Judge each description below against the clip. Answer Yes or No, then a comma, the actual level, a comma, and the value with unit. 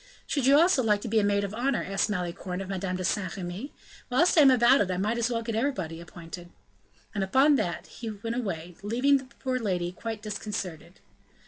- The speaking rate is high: Yes, fast, 215 wpm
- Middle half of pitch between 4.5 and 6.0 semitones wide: Yes, average, 5.1 semitones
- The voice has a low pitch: No, high, 210 Hz